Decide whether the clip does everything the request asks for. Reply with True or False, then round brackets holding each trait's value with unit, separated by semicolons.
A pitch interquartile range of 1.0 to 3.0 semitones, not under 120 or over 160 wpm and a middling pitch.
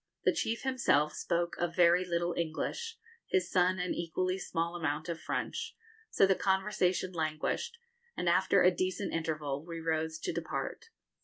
True (2.5 semitones; 155 wpm; 175 Hz)